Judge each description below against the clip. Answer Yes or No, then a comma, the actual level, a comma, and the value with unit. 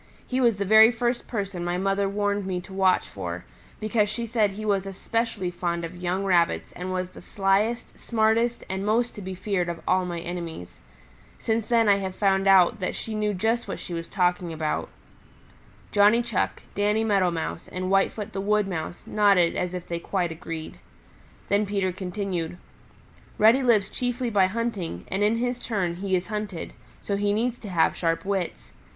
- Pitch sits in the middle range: No, high, 195 Hz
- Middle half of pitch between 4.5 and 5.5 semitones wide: No, average, 3.2 semitones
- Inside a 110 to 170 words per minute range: No, average, 185 wpm